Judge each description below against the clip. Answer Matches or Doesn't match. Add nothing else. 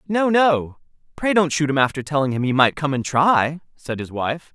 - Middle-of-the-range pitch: Matches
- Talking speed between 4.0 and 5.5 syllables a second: Matches